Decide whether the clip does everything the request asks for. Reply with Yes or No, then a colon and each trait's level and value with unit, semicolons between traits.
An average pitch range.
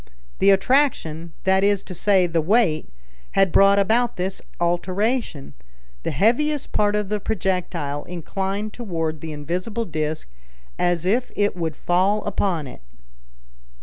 Yes: average, 3.9 semitones